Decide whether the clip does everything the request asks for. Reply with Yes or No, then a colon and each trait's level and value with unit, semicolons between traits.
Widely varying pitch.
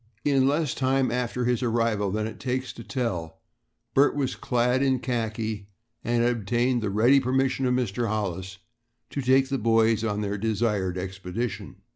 No: average, 3.5 semitones